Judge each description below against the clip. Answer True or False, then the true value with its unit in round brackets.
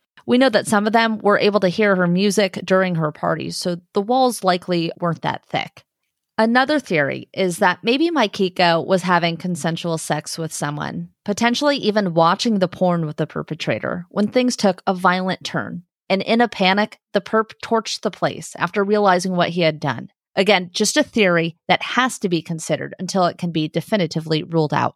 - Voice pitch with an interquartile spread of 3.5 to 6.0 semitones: True (3.9 semitones)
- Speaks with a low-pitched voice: False (185 Hz)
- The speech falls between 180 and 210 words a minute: True (190 wpm)